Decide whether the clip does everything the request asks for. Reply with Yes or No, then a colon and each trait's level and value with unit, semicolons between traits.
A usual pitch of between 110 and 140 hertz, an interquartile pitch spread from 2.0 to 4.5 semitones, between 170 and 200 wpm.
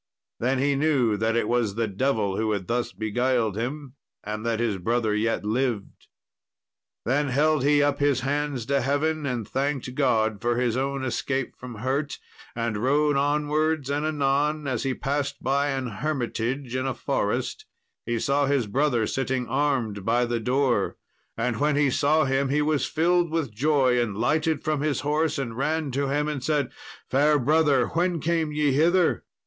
Yes: low, 135 Hz; average, 3.7 semitones; average, 175 wpm